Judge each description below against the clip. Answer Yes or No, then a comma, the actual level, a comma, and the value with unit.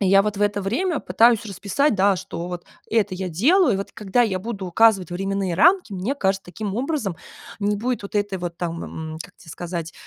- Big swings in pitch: No, average, 3.5 semitones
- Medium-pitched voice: No, high, 200 Hz